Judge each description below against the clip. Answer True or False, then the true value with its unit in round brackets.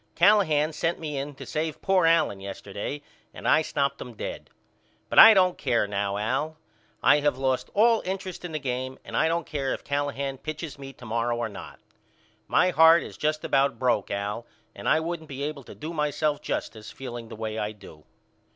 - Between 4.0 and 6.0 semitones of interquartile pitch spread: True (5.1 semitones)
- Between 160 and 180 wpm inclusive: False (195 wpm)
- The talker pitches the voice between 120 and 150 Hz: True (140 Hz)